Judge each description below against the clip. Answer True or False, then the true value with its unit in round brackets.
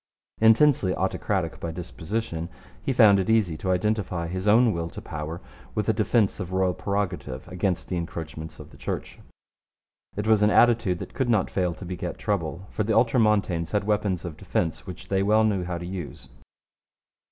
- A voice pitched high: False (95 Hz)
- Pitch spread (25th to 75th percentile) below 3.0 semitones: False (3.8 semitones)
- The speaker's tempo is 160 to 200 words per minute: True (180 wpm)